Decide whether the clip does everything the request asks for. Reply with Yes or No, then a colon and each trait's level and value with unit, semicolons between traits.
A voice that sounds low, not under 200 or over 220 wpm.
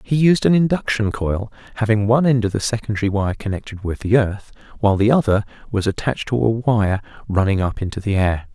Yes: low, 110 Hz; fast, 205 wpm